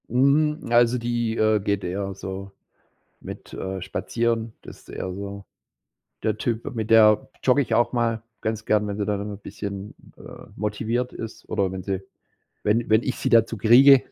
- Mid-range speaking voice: No, low, 110 Hz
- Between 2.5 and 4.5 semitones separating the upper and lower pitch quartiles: Yes, average, 2.8 semitones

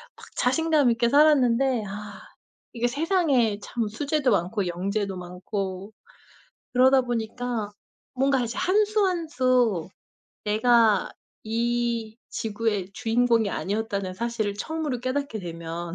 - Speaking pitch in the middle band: No, high, 230 Hz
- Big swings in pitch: No, average, 4.1 semitones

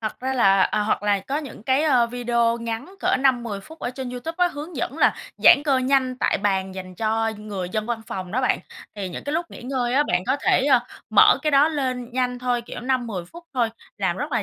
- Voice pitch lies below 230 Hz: No, high, 245 Hz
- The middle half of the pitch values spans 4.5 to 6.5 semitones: No, average, 3.7 semitones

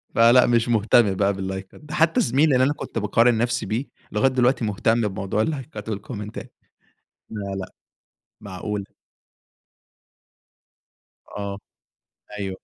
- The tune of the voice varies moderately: Yes, average, 3.5 semitones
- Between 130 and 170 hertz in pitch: No, low, 110 Hz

